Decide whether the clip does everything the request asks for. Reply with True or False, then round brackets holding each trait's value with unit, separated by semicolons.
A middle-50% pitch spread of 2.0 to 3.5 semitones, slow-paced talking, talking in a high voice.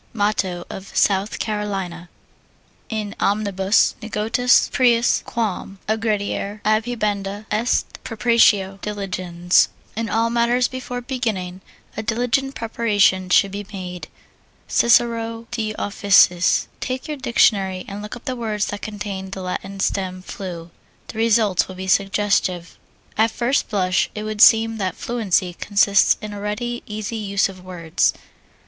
True (3.0 semitones; 130 wpm; 210 Hz)